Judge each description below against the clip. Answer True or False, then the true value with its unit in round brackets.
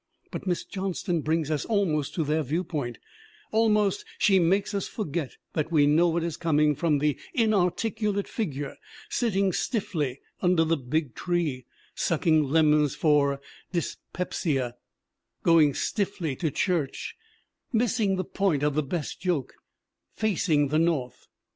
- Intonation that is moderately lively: True (4.5 semitones)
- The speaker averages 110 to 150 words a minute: True (135 wpm)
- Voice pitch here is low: False (165 Hz)